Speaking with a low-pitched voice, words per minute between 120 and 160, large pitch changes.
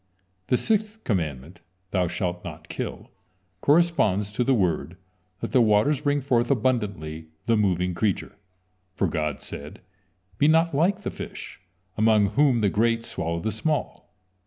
Yes: low, 110 Hz; average, 145 wpm; wide, 7.7 semitones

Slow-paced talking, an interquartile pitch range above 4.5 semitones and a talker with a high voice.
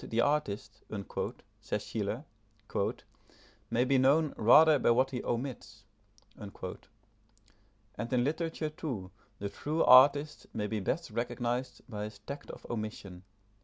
No: slow, 125 wpm; average, 4.9 semitones; low, 120 Hz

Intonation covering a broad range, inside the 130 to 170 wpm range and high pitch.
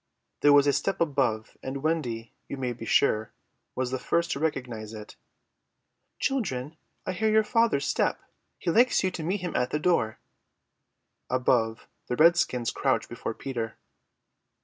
No: wide, 5.8 semitones; average, 155 wpm; medium, 140 Hz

